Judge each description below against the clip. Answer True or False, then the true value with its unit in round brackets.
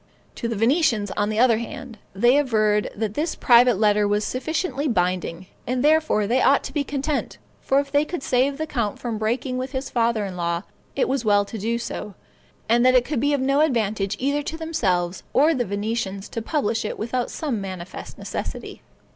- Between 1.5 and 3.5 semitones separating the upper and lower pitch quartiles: False (4.9 semitones)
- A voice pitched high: True (235 Hz)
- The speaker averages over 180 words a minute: True (200 wpm)